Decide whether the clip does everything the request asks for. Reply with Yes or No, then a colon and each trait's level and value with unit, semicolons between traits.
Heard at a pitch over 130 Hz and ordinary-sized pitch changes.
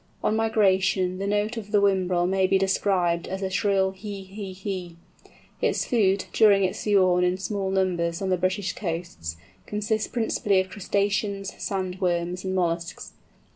No: high, 190 Hz; narrow, 1.8 semitones